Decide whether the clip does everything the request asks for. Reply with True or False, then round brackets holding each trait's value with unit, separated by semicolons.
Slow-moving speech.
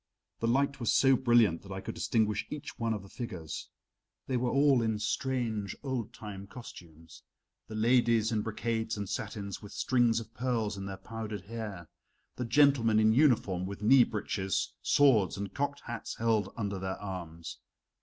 False (170 wpm)